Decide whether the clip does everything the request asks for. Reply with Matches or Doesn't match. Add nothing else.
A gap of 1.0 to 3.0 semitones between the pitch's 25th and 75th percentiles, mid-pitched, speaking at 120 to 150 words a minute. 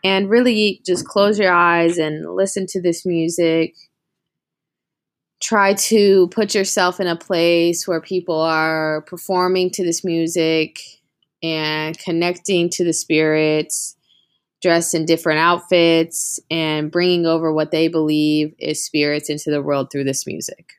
Matches